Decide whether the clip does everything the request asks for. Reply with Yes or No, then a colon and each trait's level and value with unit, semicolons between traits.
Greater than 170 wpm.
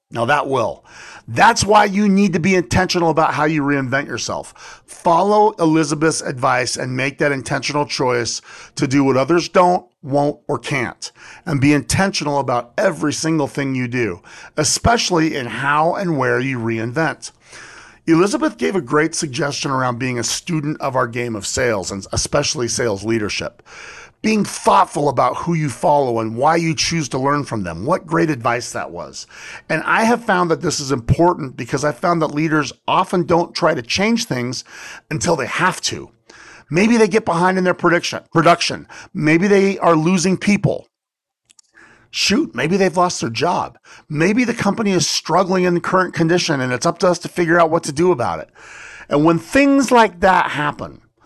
Yes: average, 180 wpm